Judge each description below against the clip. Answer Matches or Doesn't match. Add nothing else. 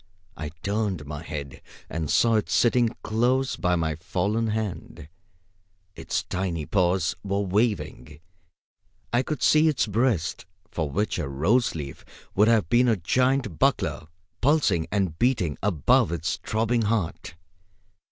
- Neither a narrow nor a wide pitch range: Doesn't match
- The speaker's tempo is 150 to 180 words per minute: Doesn't match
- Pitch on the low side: Matches